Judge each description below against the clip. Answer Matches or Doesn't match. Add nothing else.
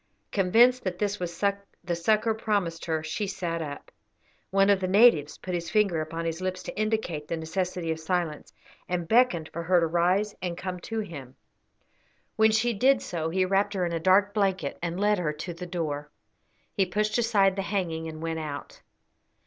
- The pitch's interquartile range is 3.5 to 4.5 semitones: Matches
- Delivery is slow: Doesn't match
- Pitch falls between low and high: Matches